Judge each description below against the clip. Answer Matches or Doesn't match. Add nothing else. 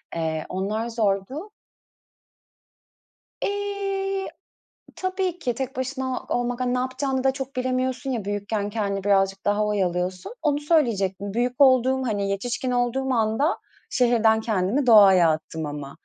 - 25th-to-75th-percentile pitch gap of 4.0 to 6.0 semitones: Matches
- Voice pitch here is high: Matches